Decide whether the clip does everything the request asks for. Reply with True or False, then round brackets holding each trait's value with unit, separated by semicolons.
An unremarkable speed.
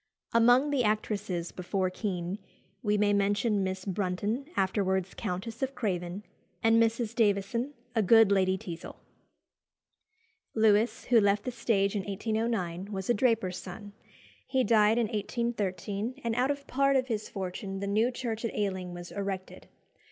True (150 wpm)